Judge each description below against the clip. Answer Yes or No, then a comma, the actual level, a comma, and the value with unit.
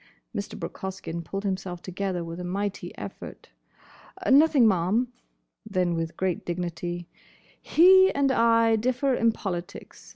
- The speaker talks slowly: Yes, slow, 130 wpm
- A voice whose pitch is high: Yes, high, 195 Hz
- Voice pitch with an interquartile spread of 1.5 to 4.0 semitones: No, average, 4.8 semitones